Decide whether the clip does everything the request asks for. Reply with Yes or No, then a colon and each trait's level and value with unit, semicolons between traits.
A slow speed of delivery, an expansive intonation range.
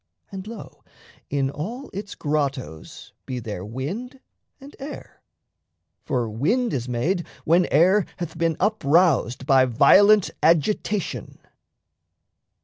Yes: slow, 110 wpm; wide, 7.7 semitones